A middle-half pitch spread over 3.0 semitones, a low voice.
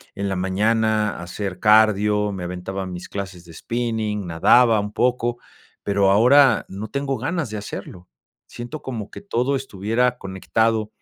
Yes: average, 3.7 semitones; low, 105 Hz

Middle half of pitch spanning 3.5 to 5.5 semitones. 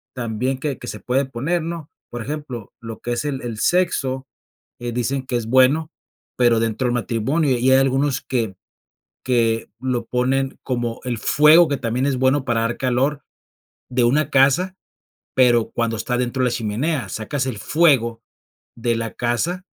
No: average, 2.7 semitones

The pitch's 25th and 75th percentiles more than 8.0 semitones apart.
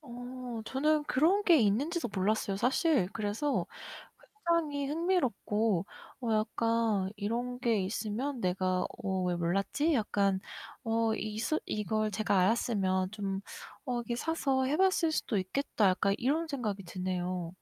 No: wide, 5.6 semitones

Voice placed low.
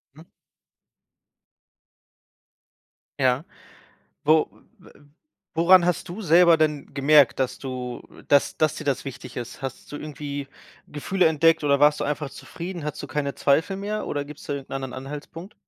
No: medium, 150 Hz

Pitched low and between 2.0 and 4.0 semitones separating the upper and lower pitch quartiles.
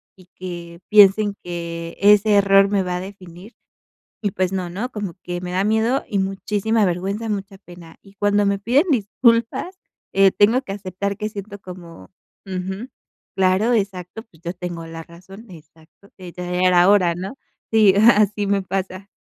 No: high, 195 Hz; narrow, 2.6 semitones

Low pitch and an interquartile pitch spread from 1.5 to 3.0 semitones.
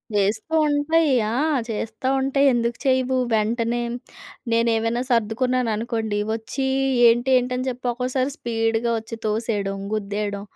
No: high, 230 Hz; narrow, 2.5 semitones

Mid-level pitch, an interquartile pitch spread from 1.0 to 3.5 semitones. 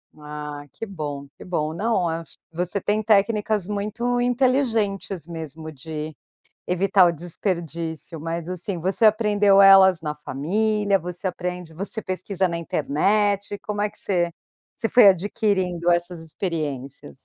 No: medium, 180 Hz; average, 4.1 semitones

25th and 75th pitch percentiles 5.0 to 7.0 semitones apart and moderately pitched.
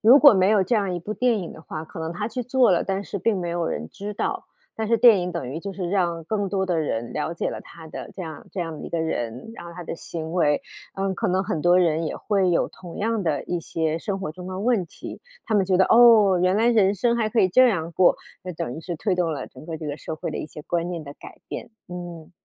No: average, 3.7 semitones; medium, 180 Hz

